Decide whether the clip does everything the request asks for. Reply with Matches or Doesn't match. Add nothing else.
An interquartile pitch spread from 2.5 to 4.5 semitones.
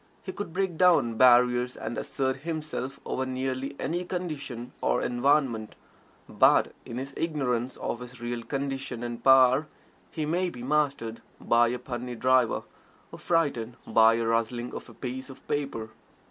Matches